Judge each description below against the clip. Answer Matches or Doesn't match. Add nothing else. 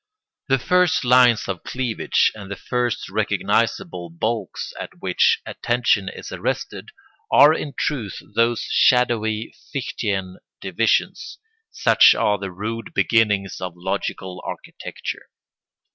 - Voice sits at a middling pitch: Doesn't match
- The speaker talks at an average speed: Doesn't match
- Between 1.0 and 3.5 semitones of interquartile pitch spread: Doesn't match